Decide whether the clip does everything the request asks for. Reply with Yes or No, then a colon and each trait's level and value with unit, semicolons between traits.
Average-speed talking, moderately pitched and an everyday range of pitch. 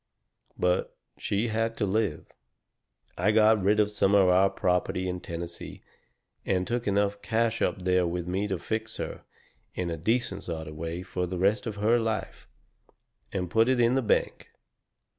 No: average, 175 wpm; low, 100 Hz; average, 3.5 semitones